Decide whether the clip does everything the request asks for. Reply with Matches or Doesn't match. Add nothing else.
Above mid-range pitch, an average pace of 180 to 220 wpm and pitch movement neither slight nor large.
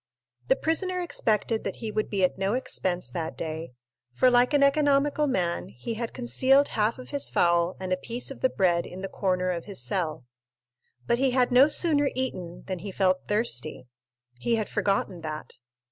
Doesn't match